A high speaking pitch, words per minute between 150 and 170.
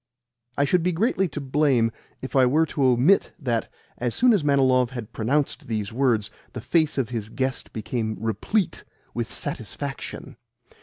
No: low, 130 Hz; average, 160 wpm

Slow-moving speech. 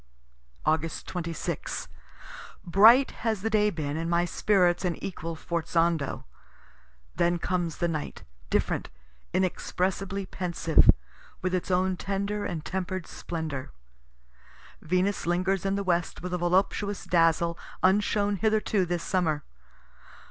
Yes: slow, 120 wpm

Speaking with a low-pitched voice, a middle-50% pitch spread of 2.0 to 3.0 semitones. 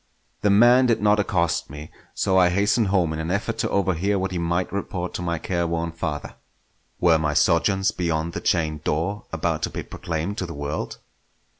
No: very low, 85 Hz; average, 3.5 semitones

